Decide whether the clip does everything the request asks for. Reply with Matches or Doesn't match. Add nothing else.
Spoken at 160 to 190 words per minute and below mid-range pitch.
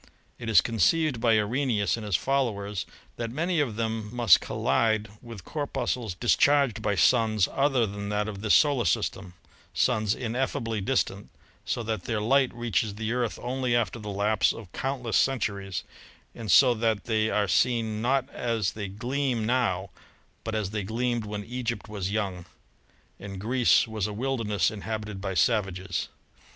Matches